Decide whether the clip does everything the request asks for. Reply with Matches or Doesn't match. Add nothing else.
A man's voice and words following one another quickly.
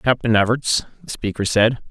Doesn't match